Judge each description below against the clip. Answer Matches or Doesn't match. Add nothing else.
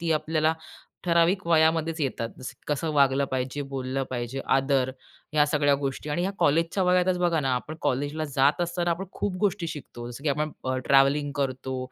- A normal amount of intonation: Matches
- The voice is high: Doesn't match